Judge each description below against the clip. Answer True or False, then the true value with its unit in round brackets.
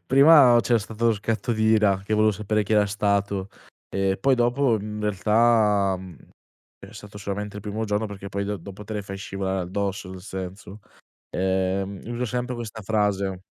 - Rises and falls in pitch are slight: True (2.1 semitones)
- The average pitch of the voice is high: False (105 Hz)